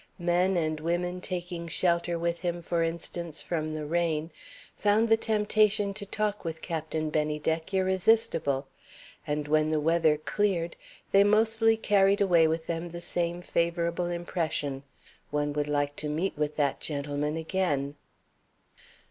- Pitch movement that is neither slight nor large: Yes, average, 3.5 semitones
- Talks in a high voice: No, medium, 170 Hz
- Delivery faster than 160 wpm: No, average, 140 wpm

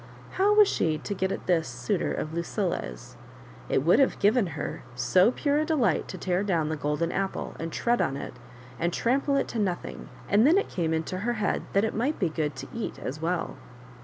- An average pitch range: No, wide, 6.8 semitones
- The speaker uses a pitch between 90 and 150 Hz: No, medium, 185 Hz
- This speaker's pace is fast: Yes, fast, 215 wpm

